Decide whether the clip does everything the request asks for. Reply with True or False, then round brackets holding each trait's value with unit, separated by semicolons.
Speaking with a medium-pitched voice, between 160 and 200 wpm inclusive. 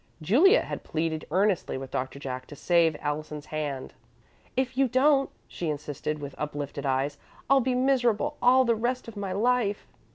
True (175 Hz; 165 wpm)